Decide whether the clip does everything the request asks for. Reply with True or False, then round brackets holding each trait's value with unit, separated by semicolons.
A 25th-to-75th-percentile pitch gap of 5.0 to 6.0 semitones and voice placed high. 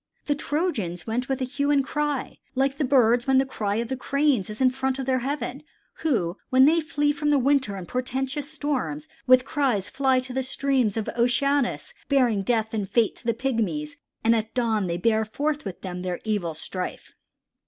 False (4.2 semitones; 255 Hz)